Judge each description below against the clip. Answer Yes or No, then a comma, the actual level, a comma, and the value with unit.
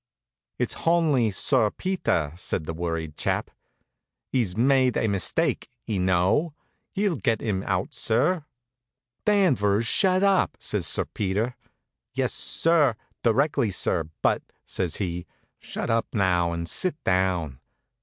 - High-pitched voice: No, low, 110 Hz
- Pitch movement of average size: No, wide, 8.3 semitones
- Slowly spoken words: Yes, slow, 130 wpm